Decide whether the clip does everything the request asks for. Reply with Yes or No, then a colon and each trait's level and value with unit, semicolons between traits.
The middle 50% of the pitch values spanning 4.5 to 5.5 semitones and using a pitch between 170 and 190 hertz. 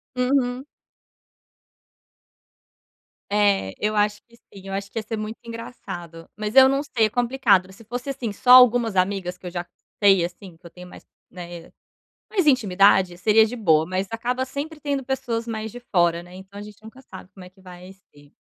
No: average, 4.9 semitones; high, 210 Hz